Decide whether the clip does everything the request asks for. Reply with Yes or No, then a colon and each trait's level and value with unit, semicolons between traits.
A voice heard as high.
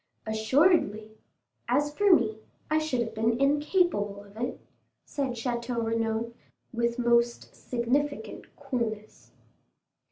Yes: high, 235 Hz